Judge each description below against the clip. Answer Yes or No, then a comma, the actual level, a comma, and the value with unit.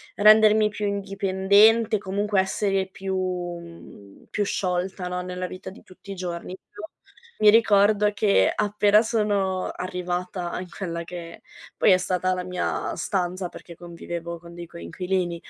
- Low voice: No, medium, 185 Hz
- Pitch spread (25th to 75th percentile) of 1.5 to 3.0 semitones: Yes, narrow, 2.3 semitones